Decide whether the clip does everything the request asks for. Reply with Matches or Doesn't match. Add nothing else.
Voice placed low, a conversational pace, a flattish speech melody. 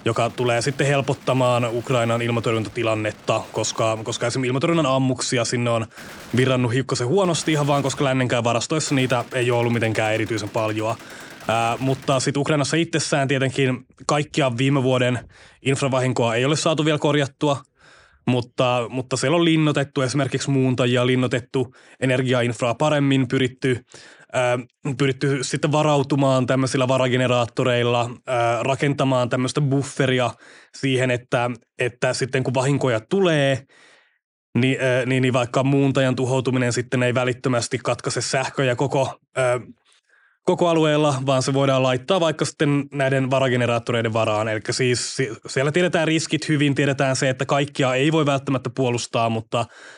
Doesn't match